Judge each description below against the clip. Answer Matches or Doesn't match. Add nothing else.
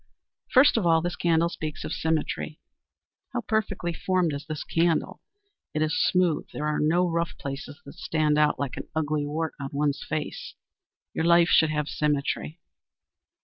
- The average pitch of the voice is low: Doesn't match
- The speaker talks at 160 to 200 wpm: Matches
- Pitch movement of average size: Doesn't match